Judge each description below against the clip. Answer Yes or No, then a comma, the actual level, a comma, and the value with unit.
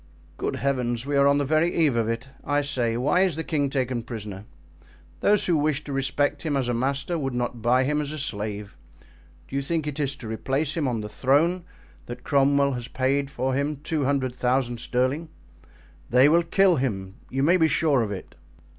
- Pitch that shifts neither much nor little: Yes, average, 3.3 semitones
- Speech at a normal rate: No, fast, 210 wpm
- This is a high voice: No, low, 135 Hz